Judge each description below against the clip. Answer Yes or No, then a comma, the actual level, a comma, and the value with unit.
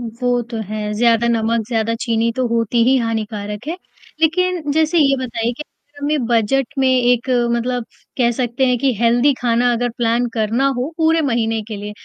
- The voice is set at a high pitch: Yes, high, 240 Hz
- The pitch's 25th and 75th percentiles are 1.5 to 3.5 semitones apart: Yes, average, 2.8 semitones